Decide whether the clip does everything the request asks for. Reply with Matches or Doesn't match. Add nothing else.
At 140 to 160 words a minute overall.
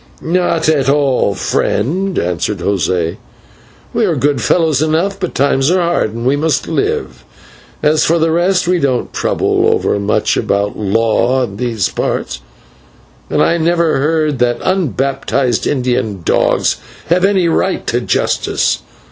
Matches